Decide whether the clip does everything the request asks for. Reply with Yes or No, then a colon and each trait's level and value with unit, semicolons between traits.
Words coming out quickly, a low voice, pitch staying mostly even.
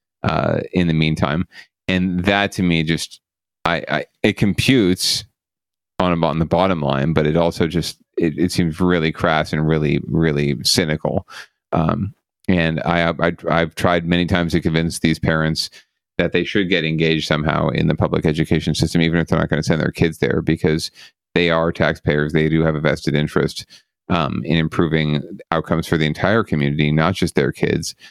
No: average, 185 wpm; very low, 80 Hz; narrow, 1.8 semitones